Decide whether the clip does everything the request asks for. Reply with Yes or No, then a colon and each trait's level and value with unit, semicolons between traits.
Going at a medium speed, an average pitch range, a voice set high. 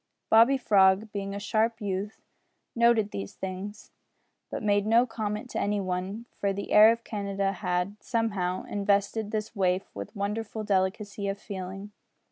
No: average, 150 wpm; narrow, 2.0 semitones; high, 205 Hz